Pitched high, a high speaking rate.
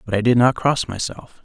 No: low, 115 Hz; fast, 250 wpm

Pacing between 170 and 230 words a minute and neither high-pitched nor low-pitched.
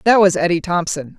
Yes: fast, 205 wpm; medium, 180 Hz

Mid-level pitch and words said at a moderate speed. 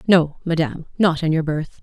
Yes: medium, 160 Hz; average, 195 wpm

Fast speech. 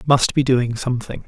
No: average, 190 wpm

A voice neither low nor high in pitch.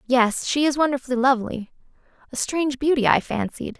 No: very high, 265 Hz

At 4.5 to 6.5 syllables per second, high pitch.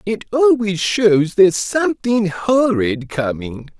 No: 3.7 syllables/s; high, 195 Hz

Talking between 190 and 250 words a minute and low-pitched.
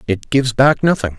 Yes: fast, 205 wpm; low, 125 Hz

